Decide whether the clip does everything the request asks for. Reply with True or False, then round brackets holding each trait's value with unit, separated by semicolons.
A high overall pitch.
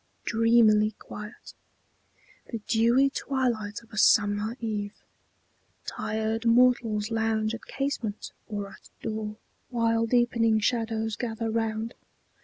True (225 Hz)